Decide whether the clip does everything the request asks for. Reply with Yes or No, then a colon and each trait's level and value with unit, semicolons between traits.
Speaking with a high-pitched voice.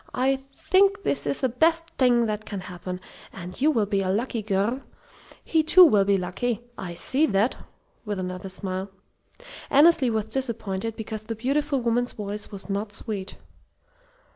Yes: high, 220 Hz